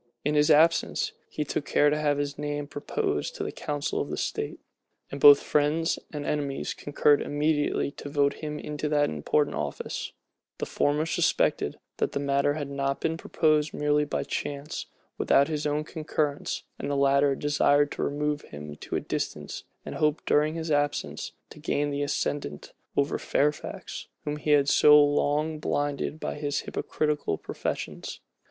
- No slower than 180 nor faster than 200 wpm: No, average, 160 wpm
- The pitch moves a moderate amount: No, narrow, 0.9 semitones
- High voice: No, medium, 145 Hz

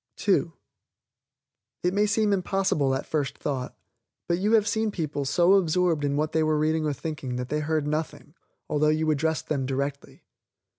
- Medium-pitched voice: Yes, medium, 155 Hz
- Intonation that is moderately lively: Yes, average, 3.8 semitones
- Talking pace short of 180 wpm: Yes, average, 170 wpm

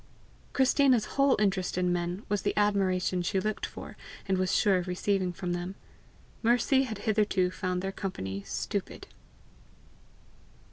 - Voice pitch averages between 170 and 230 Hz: Yes, high, 190 Hz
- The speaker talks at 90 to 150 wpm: Yes, average, 140 wpm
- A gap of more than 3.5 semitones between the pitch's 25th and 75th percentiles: No, average, 2.8 semitones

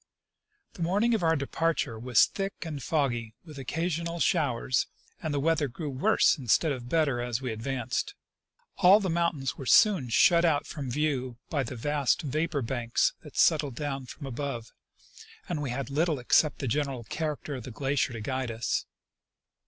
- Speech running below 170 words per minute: No, average, 175 wpm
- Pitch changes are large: No, average, 4.4 semitones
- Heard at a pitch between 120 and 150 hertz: Yes, medium, 140 Hz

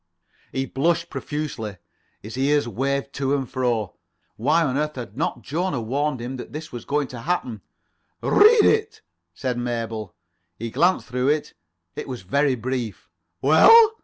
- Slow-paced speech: No, average, 155 wpm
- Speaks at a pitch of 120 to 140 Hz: Yes, low, 135 Hz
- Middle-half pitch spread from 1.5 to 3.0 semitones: No, average, 4.1 semitones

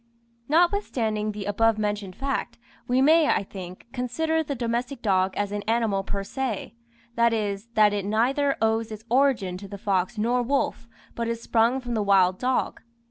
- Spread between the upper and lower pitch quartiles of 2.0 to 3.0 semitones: No, average, 3.8 semitones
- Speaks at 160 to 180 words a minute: Yes, average, 175 wpm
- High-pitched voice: Yes, high, 225 Hz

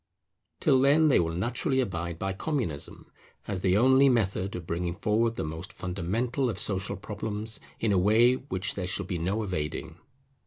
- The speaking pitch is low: Yes, low, 100 Hz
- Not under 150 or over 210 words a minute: Yes, average, 170 wpm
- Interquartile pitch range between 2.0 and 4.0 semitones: No, average, 4.9 semitones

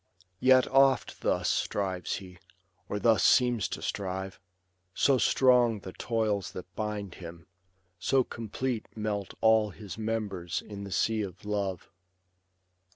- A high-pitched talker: No, low, 105 Hz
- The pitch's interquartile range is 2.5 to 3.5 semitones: Yes, average, 3.1 semitones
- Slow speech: Yes, slow, 130 wpm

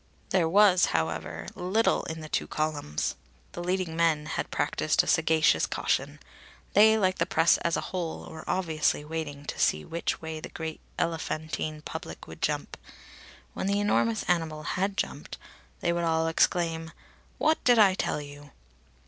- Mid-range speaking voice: Yes, medium, 165 Hz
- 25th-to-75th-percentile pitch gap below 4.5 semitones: Yes, average, 2.9 semitones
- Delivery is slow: No, average, 160 wpm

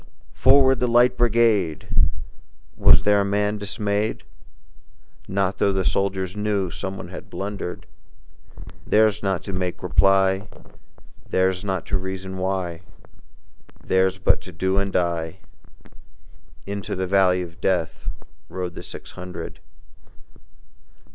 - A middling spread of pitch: No, narrow, 1.8 semitones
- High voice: No, very low, 95 Hz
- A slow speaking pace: Yes, slow, 130 wpm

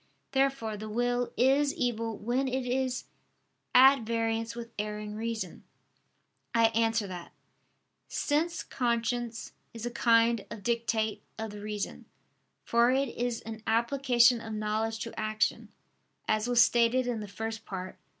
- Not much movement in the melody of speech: Yes, narrow, 1.9 semitones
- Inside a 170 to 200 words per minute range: No, average, 140 wpm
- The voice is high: Yes, high, 230 Hz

